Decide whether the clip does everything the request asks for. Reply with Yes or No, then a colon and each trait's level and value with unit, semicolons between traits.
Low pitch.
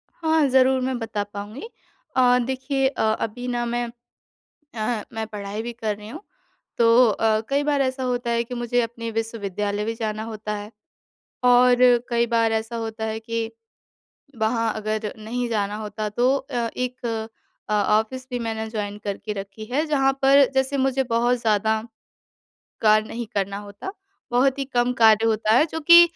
No: high, 230 Hz